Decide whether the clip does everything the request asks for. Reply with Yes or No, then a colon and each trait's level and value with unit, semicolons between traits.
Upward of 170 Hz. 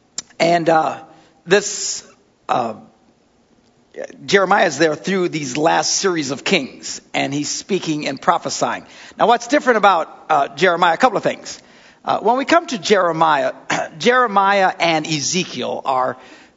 Yes: medium, 185 Hz